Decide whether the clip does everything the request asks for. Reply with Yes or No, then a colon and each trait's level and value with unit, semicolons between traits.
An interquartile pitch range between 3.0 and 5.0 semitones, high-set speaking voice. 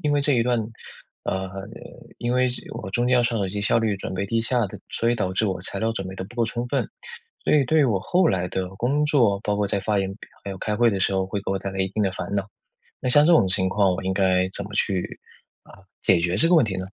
No: average, 4.1 semitones; low, 105 Hz